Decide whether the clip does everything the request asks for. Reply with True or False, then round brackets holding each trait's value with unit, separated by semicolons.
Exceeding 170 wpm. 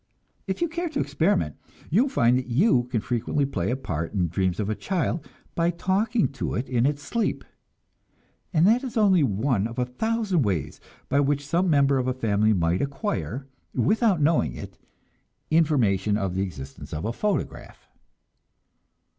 True (180 wpm)